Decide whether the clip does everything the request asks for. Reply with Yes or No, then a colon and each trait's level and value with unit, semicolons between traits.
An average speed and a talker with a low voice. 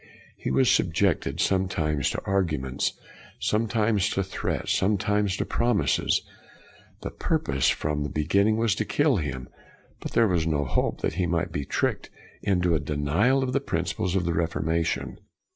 Yes: average, 155 wpm; very low, 90 Hz